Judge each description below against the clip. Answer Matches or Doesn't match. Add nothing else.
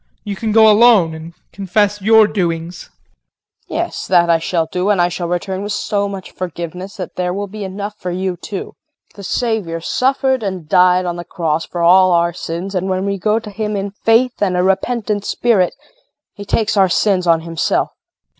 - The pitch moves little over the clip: Doesn't match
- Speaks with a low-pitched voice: Doesn't match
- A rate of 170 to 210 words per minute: Matches